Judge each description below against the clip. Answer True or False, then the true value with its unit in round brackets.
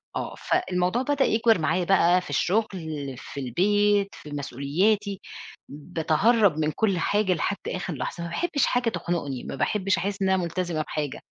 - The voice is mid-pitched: True (180 Hz)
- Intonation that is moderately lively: True (4.9 semitones)